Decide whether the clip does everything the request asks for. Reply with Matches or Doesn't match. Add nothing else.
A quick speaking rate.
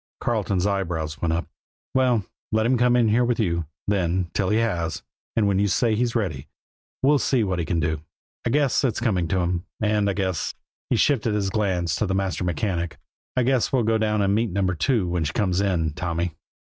Matches